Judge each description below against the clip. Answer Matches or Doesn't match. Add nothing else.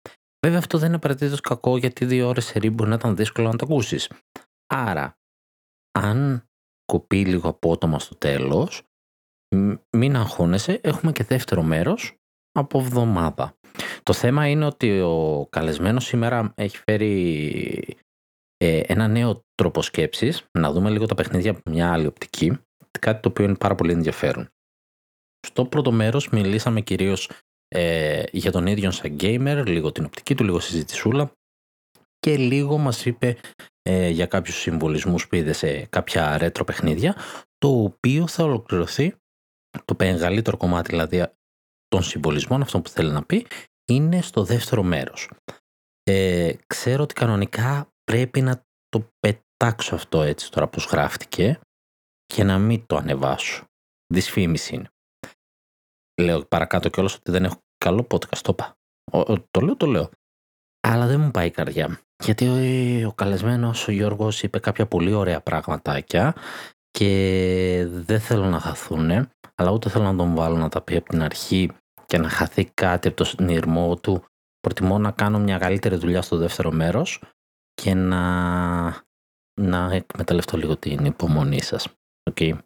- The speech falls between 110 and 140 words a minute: Doesn't match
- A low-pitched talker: Matches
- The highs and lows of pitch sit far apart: Matches